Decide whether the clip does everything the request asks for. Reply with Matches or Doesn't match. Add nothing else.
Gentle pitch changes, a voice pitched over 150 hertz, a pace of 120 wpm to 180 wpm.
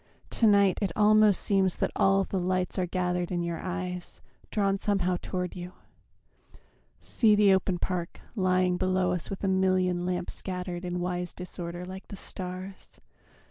Matches